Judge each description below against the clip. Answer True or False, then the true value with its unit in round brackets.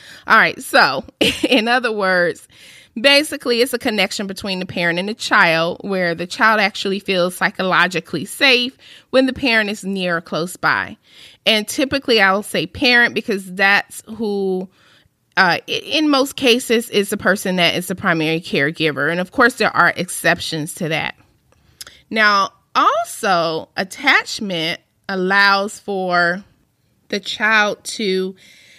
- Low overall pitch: False (195 Hz)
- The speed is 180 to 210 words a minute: False (140 wpm)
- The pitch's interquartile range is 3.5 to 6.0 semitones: True (4.5 semitones)